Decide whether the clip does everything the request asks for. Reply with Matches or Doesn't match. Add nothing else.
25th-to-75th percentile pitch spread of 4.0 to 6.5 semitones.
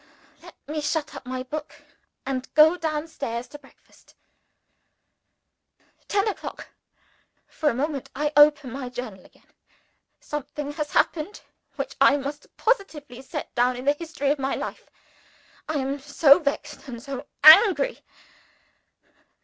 Doesn't match